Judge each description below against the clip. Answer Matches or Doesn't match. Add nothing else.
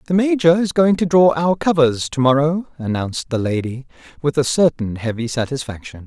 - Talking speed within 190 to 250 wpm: Doesn't match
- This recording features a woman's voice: Doesn't match